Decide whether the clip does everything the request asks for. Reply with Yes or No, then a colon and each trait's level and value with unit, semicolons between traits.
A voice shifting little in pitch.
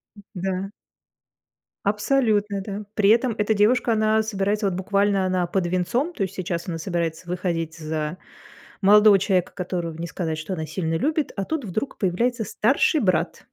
No: average, 3.5 semitones